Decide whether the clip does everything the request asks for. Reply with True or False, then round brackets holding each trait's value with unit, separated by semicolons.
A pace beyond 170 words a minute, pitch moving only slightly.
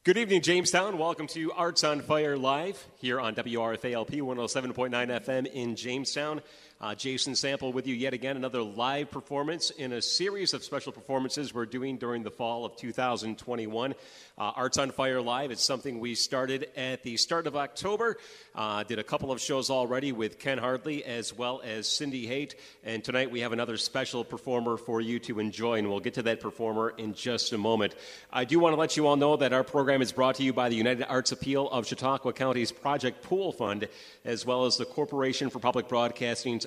False (200 wpm; 3.0 semitones)